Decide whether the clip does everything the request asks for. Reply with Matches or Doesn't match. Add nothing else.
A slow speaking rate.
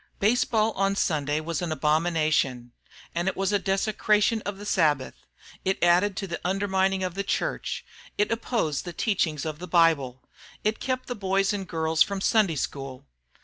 Doesn't match